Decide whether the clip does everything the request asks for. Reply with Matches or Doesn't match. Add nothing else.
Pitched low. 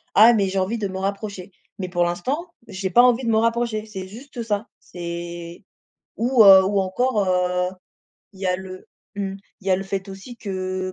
Doesn't match